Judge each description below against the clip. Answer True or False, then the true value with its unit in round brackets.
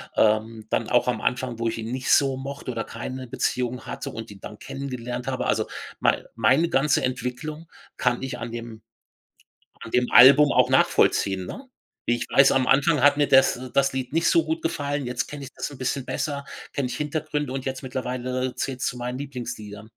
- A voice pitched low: True (130 Hz)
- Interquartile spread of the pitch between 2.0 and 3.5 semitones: True (2.4 semitones)